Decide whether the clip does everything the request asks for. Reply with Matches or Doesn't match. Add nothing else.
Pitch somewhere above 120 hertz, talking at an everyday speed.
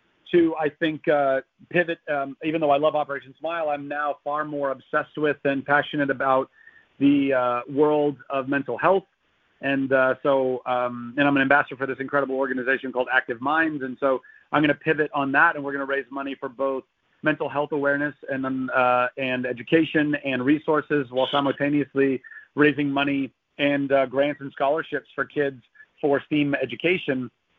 Matches